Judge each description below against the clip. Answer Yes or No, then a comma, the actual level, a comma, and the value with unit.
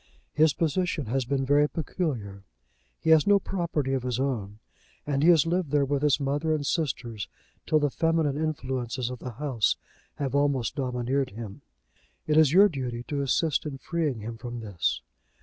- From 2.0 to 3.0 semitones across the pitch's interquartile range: No, average, 3.9 semitones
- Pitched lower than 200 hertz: Yes, medium, 140 Hz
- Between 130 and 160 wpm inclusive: No, average, 175 wpm